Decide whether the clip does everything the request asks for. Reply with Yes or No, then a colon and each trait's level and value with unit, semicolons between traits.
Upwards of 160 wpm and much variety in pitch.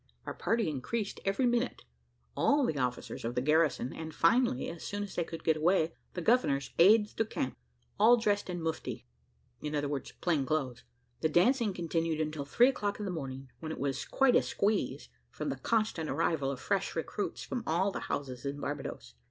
Yes: average, 185 wpm; wide, 6.5 semitones